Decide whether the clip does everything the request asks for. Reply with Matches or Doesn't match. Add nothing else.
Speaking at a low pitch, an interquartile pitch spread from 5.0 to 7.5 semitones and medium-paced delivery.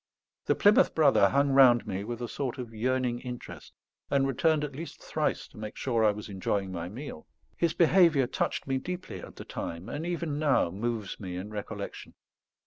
Matches